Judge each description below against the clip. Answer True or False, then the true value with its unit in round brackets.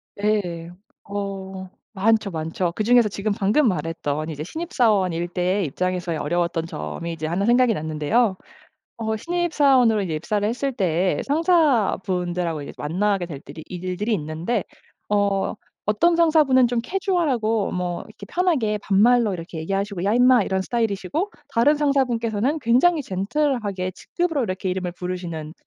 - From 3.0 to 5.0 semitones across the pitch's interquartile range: False (5.5 semitones)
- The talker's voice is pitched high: True (200 Hz)